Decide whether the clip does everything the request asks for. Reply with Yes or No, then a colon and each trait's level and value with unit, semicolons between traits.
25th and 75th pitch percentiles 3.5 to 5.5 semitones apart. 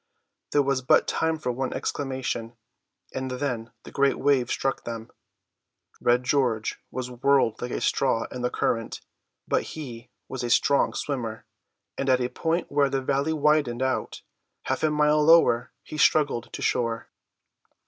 No: average, 3.0 semitones